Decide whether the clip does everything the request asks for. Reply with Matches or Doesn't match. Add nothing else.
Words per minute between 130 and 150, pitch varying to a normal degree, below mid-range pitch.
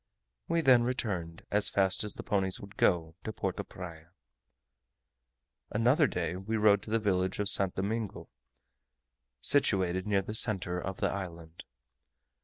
Matches